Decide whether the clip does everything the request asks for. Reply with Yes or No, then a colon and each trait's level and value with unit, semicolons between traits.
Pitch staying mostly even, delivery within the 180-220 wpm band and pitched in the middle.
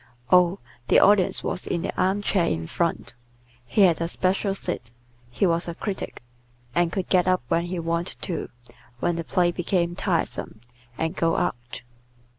No: narrow, 1.8 semitones; average, 170 wpm; medium, 175 Hz